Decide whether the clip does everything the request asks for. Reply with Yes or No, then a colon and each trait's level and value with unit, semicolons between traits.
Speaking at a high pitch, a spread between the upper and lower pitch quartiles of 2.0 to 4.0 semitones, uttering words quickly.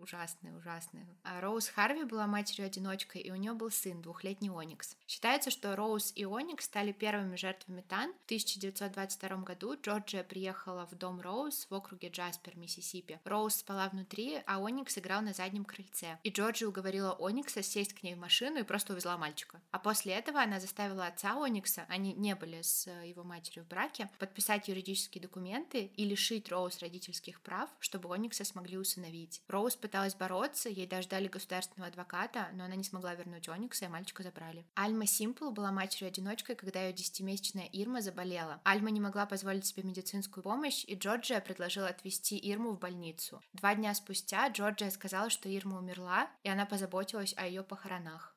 Yes: high, 195 Hz; narrow, 2.4 semitones; fast, 170 wpm